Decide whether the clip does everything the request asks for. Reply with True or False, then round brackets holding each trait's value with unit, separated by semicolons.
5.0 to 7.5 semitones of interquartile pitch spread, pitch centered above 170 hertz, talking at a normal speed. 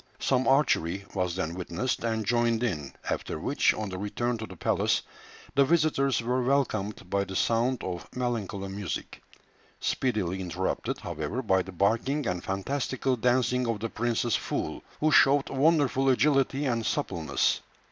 False (5.3 semitones; 115 Hz; 150 wpm)